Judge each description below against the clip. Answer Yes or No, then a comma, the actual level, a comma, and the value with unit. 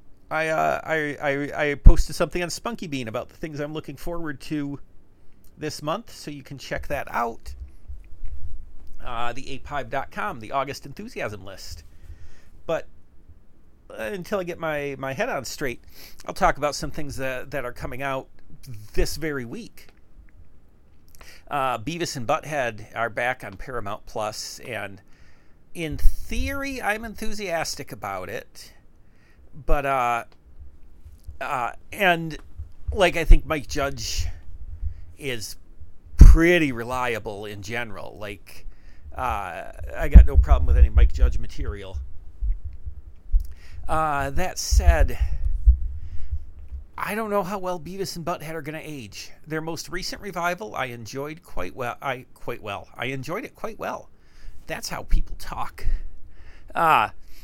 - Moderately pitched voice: No, low, 110 Hz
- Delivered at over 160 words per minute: No, average, 140 wpm